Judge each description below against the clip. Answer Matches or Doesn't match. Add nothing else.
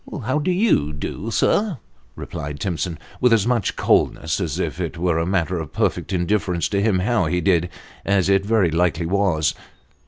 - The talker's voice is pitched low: Matches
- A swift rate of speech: Doesn't match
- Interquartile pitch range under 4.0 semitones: Doesn't match